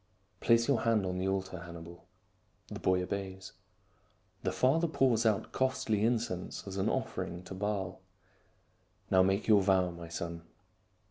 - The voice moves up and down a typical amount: Yes, average, 3.6 semitones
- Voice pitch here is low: Yes, very low, 95 Hz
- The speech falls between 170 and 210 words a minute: No, average, 155 wpm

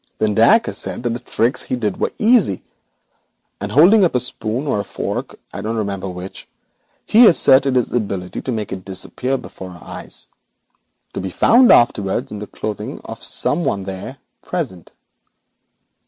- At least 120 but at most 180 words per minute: Yes, average, 165 wpm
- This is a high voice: No, low, 110 Hz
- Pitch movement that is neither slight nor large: No, wide, 5.7 semitones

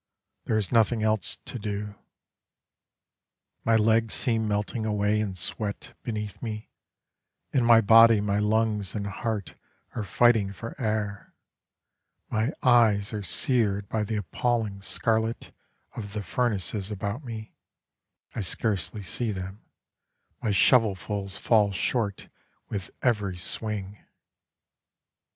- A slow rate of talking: Yes, slow, 120 wpm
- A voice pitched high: No, low, 105 Hz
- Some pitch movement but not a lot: No, narrow, 2.0 semitones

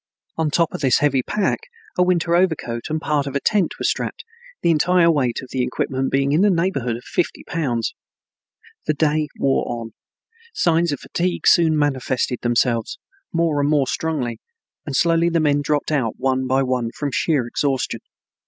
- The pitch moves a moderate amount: Yes, average, 4.2 semitones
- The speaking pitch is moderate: Yes, medium, 145 Hz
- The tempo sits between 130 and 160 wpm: No, average, 180 wpm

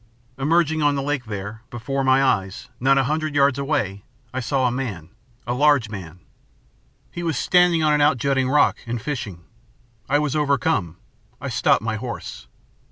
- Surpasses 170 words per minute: No, average, 165 wpm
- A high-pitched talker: No, low, 135 Hz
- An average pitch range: Yes, average, 4.7 semitones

